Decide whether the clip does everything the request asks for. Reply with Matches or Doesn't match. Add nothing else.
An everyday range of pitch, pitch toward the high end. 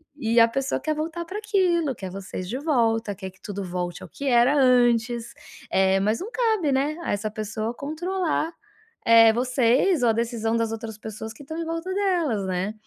Doesn't match